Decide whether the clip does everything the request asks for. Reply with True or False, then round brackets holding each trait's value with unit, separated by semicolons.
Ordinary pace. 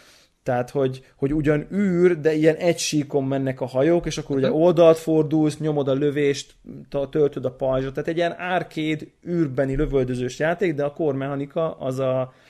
False (165 wpm)